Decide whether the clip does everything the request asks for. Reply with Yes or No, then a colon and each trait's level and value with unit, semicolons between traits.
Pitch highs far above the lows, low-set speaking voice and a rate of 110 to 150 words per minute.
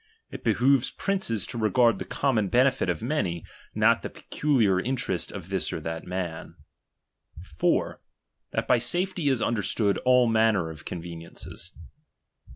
Yes: wide, 6.0 semitones; low, 110 Hz; average, 140 wpm